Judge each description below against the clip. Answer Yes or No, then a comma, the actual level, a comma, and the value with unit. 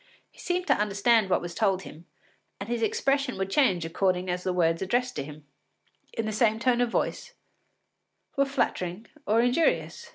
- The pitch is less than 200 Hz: No, high, 215 Hz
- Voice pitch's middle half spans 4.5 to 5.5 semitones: Yes, average, 5.2 semitones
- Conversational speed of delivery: Yes, average, 175 wpm